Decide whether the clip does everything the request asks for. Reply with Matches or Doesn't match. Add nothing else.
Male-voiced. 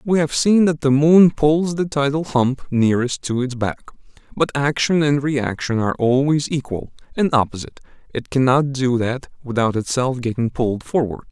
Matches